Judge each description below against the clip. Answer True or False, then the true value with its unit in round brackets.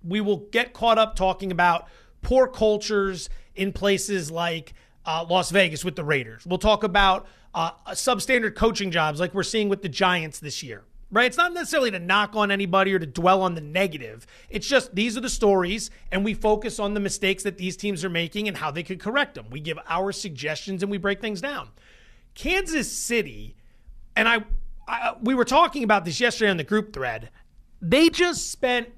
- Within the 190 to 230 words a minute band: True (200 wpm)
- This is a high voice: True (200 Hz)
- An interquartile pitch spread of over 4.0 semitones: False (3.7 semitones)